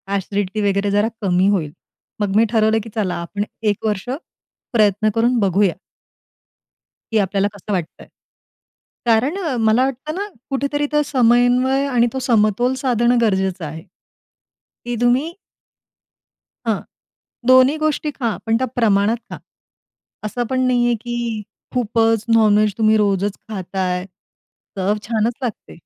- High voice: Yes, high, 220 Hz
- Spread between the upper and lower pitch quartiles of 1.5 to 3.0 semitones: No, average, 3.4 semitones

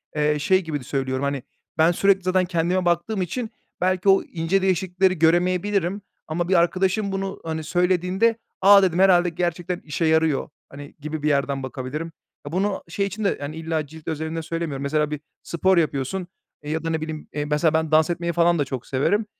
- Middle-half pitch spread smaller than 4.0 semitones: Yes, average, 3.4 semitones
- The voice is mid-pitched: Yes, medium, 170 Hz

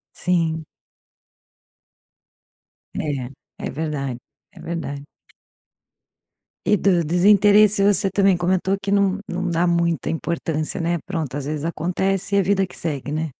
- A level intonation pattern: No, average, 3.6 semitones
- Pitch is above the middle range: No, medium, 175 Hz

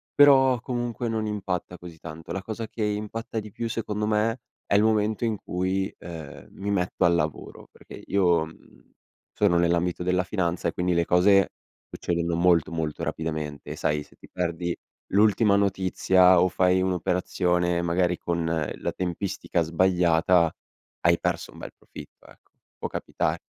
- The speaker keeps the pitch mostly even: No, average, 3.3 semitones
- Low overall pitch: Yes, very low, 90 Hz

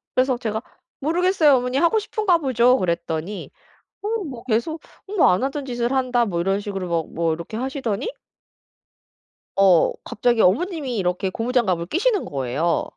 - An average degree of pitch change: No, wide, 7.1 semitones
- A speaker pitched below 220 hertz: No, high, 240 Hz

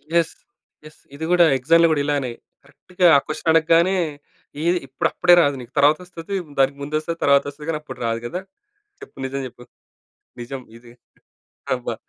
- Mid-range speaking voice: Yes, medium, 150 Hz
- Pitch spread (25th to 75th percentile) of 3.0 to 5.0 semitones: Yes, average, 3.6 semitones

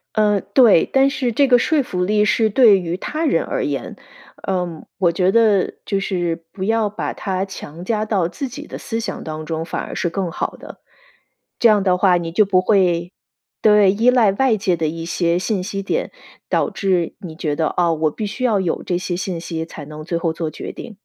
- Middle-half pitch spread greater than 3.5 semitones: Yes, average, 4.2 semitones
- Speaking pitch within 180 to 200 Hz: Yes, high, 190 Hz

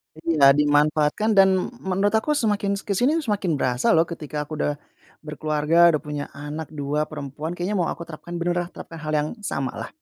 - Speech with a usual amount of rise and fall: Yes, average, 4.1 semitones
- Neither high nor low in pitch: Yes, medium, 160 Hz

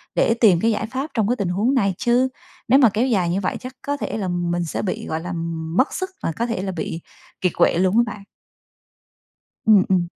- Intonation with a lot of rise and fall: No, average, 4.9 semitones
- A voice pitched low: No, high, 205 Hz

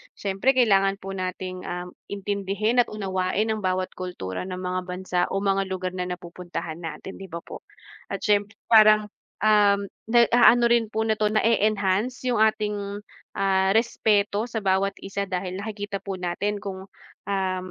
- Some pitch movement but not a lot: No, narrow, 2.3 semitones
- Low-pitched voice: No, high, 195 Hz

